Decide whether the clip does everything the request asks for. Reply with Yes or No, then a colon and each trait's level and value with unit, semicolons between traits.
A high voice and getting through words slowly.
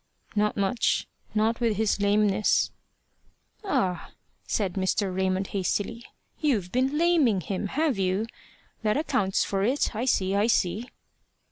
Yes: high, 210 Hz; slow, 130 wpm